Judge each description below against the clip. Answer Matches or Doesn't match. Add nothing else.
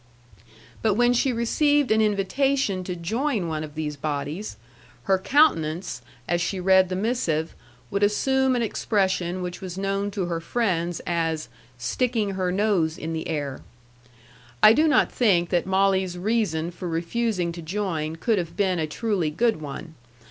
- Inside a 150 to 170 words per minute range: Matches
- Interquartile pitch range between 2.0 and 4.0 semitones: Doesn't match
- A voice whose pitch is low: Doesn't match